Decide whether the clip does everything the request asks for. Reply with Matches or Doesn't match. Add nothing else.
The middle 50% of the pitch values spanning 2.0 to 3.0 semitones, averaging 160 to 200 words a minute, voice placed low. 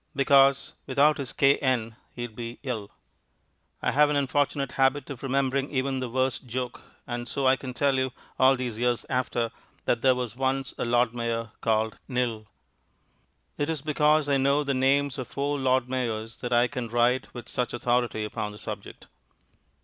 Matches